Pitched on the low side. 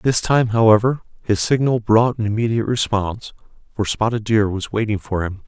Yes: low, 110 Hz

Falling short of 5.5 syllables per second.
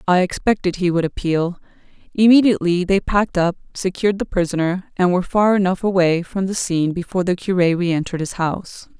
No: 6.0 syllables/s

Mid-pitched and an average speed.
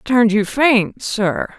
No: high, 225 Hz; average, 150 wpm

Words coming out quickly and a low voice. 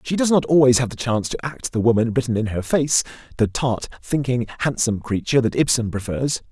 Yes: fast, 210 wpm; low, 125 Hz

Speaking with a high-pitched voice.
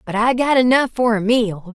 Yes: high, 230 Hz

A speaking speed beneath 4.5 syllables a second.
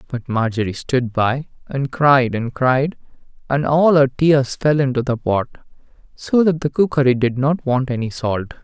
Yes: 4.3 syllables/s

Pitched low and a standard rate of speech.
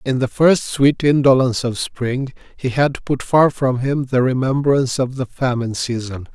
Yes: low, 130 Hz; average, 180 wpm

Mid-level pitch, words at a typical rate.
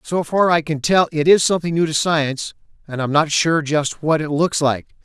No: medium, 155 Hz; fast, 250 wpm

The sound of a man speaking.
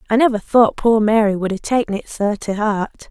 No: female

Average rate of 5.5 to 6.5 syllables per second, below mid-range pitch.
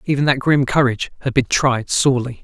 Yes: 6.0 syllables/s; low, 130 Hz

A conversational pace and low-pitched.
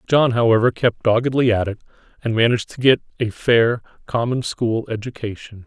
Yes: average, 160 wpm; low, 115 Hz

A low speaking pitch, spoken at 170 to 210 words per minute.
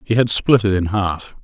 No: low, 105 Hz; fast, 250 wpm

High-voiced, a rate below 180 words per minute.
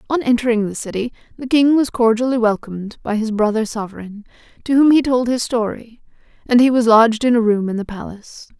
No: high, 230 Hz; average, 200 wpm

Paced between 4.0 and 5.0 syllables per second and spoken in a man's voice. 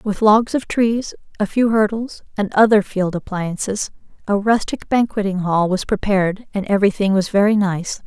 No: 4.9 syllables/s; female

